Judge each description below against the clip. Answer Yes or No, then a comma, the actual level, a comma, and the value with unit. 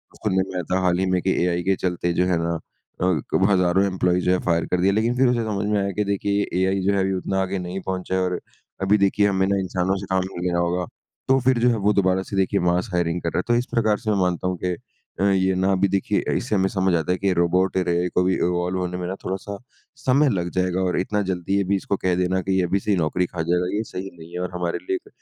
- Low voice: Yes, very low, 95 Hz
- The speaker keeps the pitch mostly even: Yes, narrow, 1.7 semitones